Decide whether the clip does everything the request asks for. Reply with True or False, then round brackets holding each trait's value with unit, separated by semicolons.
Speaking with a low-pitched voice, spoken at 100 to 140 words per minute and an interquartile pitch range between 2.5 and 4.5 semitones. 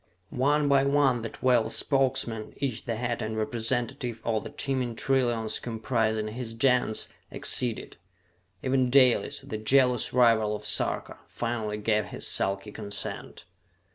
True (120 Hz; 135 wpm; 2.9 semitones)